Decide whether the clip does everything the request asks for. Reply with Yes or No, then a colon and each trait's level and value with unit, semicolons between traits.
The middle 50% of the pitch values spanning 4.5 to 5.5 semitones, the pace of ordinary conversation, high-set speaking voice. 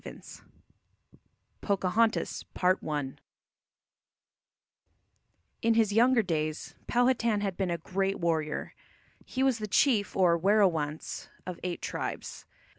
No: average, 5.0 semitones; slow, 100 wpm; high, 195 Hz